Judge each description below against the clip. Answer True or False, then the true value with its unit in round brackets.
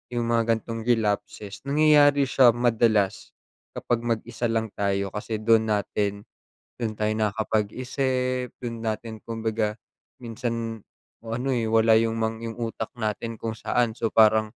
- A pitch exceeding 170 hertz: False (115 Hz)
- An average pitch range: False (1.6 semitones)